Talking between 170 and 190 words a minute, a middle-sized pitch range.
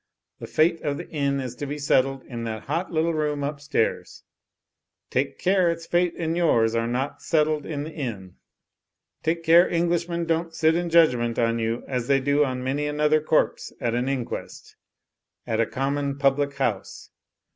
Yes: average, 180 wpm; average, 4.2 semitones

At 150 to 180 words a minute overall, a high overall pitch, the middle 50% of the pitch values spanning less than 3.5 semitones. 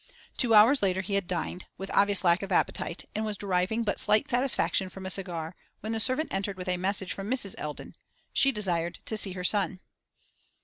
No: fast, 205 wpm; high, 195 Hz; average, 2.8 semitones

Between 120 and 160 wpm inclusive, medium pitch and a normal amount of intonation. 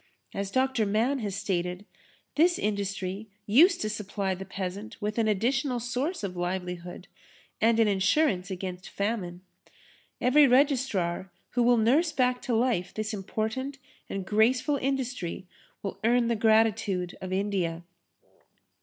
No: slow, 135 wpm; high, 215 Hz; average, 4.6 semitones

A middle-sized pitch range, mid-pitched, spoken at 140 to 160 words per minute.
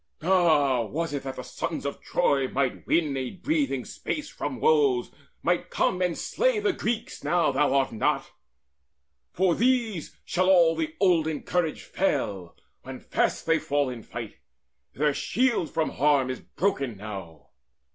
No: wide, 6.2 semitones; medium, 160 Hz; average, 155 wpm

